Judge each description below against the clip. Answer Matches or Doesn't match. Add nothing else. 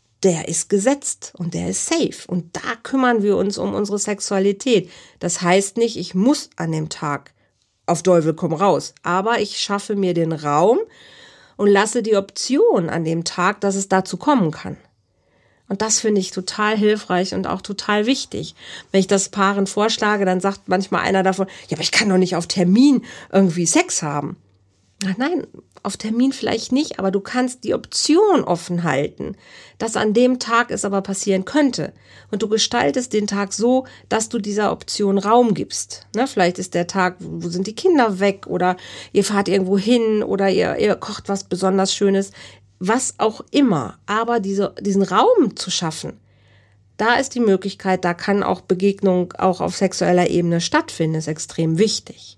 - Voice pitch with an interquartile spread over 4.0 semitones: Doesn't match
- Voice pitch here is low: Doesn't match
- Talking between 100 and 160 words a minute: Doesn't match